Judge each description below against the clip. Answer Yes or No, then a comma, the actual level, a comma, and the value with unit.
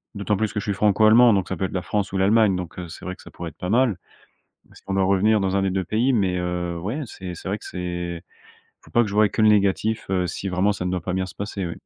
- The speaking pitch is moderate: No, very low, 95 Hz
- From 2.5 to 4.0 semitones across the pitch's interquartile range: Yes, average, 2.8 semitones